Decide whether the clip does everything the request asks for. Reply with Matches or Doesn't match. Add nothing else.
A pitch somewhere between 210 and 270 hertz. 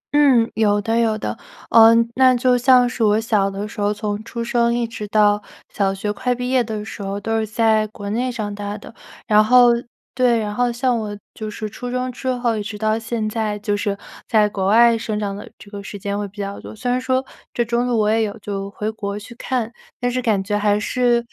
Matches